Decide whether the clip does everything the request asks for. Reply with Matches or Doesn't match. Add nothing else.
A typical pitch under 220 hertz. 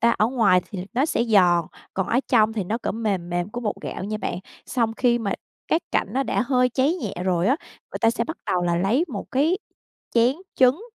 Doesn't match